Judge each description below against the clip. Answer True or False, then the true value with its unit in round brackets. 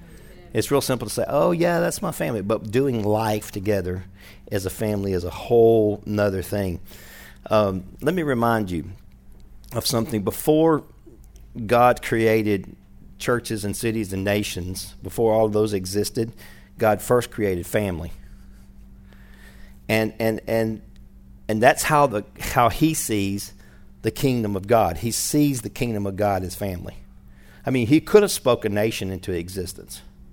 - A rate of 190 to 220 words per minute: False (155 wpm)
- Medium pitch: False (105 Hz)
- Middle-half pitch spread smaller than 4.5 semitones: True (2.9 semitones)